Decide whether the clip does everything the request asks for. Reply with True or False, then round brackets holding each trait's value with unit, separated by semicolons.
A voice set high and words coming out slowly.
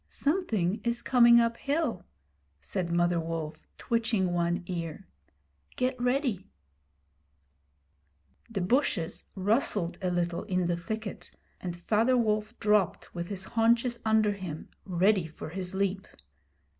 True (195 Hz; 120 wpm)